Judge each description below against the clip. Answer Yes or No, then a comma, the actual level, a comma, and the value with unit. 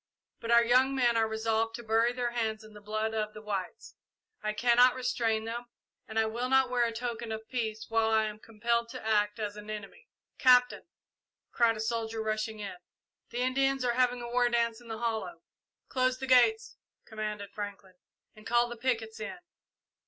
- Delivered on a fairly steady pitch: Yes, narrow, 1.9 semitones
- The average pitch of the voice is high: Yes, high, 225 Hz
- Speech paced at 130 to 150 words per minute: No, average, 190 wpm